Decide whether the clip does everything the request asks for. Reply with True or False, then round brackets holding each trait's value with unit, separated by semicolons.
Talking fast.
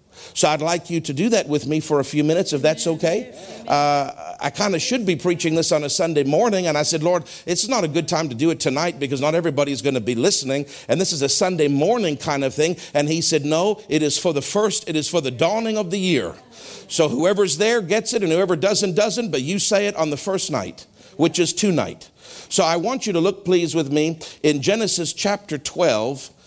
True (245 wpm)